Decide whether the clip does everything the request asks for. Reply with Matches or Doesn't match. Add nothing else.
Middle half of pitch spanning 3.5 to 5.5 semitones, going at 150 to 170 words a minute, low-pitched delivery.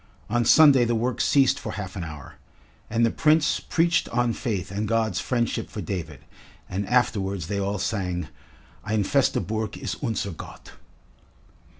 Matches